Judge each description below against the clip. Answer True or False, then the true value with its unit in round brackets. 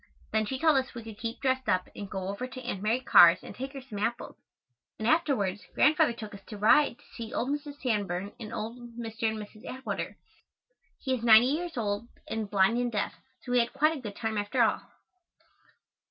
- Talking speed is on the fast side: True (210 wpm)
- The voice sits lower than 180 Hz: False (230 Hz)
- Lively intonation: False (3.8 semitones)